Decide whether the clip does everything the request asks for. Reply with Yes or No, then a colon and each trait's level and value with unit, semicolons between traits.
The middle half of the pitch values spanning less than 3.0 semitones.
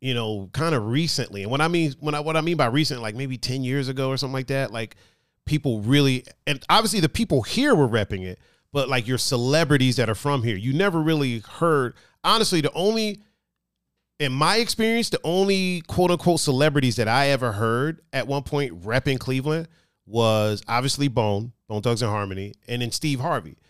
No: average, 4.5 semitones